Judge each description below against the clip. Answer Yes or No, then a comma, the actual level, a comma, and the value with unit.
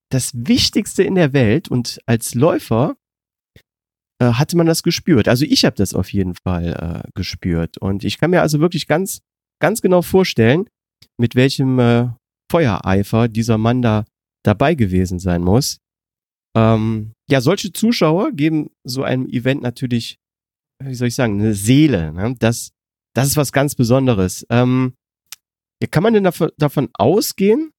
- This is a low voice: Yes, low, 125 Hz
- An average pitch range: No, wide, 5.8 semitones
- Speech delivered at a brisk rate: No, average, 160 wpm